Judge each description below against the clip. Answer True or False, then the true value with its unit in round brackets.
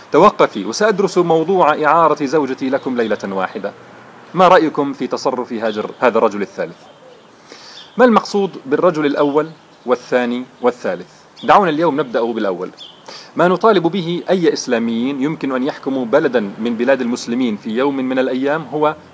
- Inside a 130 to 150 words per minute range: True (135 wpm)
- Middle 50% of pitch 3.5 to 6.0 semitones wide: True (5.0 semitones)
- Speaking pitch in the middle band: True (145 Hz)